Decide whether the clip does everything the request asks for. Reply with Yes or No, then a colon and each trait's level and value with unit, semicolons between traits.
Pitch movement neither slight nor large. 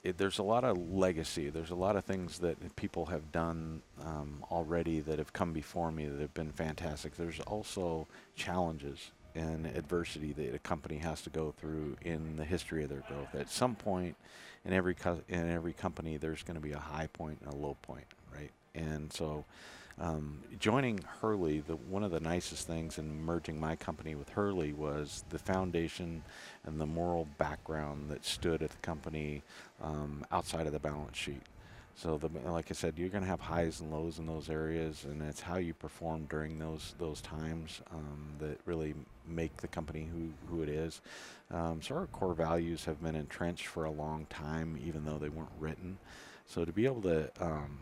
No: narrow, 2.0 semitones